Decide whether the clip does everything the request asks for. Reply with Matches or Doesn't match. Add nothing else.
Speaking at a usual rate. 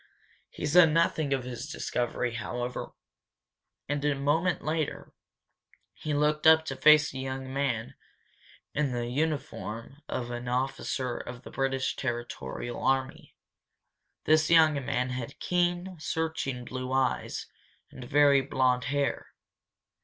Doesn't match